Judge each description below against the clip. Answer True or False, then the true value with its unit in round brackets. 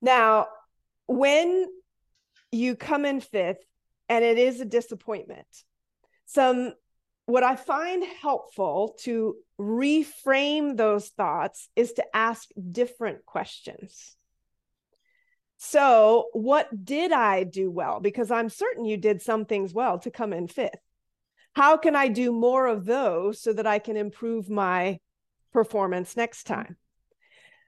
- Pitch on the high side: True (235 Hz)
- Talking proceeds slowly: True (130 wpm)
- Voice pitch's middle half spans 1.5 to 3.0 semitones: False (5.0 semitones)